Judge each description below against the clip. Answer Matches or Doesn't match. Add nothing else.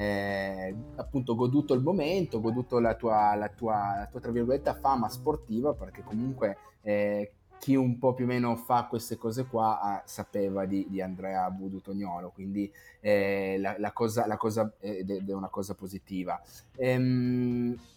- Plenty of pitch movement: Doesn't match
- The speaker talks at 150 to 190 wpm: Matches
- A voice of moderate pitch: Doesn't match